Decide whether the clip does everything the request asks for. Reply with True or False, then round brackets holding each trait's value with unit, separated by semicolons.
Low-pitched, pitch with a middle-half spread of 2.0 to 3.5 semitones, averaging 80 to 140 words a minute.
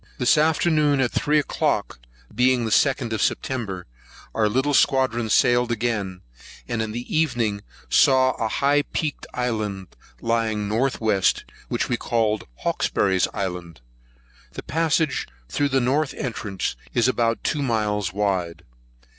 False (120 Hz; 4.2 semitones; 135 wpm)